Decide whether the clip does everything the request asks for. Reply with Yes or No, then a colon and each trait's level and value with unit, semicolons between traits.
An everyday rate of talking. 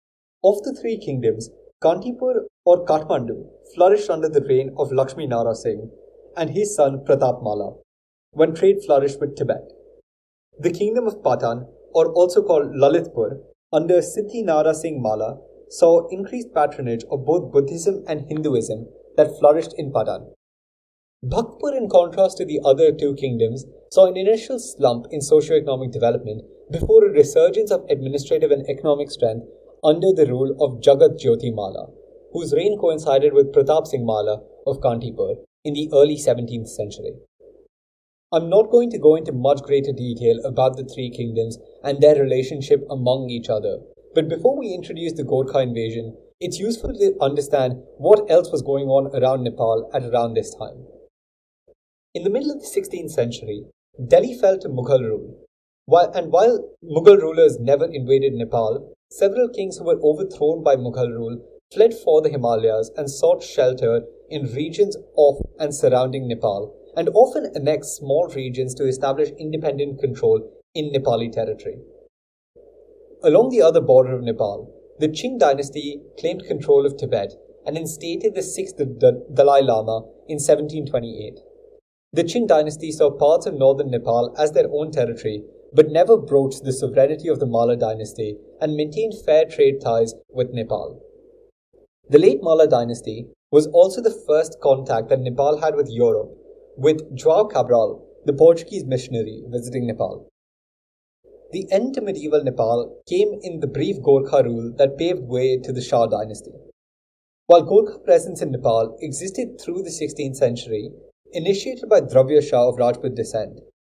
Yes: average, 155 wpm